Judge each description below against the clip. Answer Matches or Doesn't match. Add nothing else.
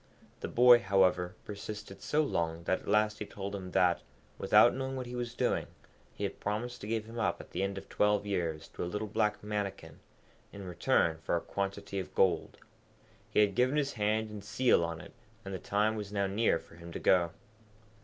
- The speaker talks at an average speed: Doesn't match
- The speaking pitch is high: Doesn't match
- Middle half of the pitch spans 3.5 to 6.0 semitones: Doesn't match